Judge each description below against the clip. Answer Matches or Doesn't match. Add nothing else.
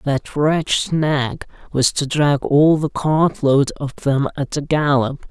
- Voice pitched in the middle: Matches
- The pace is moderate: Matches